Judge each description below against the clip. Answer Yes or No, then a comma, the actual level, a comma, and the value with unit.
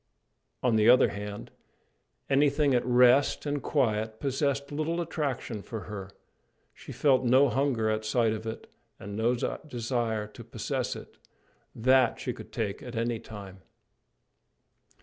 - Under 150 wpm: Yes, average, 140 wpm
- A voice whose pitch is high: No, low, 120 Hz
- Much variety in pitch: No, average, 3.9 semitones